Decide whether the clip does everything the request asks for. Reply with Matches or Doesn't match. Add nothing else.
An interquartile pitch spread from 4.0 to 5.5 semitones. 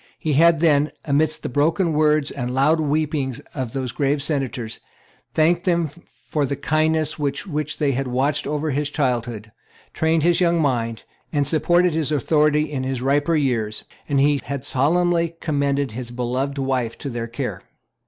Doesn't match